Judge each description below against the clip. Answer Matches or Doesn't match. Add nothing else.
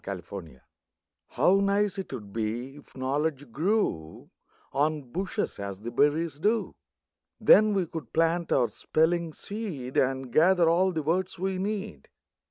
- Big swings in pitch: Matches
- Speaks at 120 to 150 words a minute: Matches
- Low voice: Doesn't match